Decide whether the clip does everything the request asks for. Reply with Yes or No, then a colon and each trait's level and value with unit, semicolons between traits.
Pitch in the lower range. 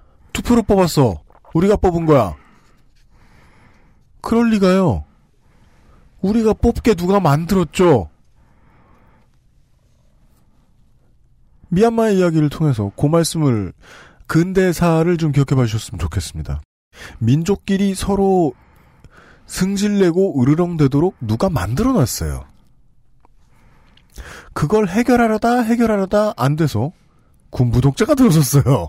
No: medium, 160 Hz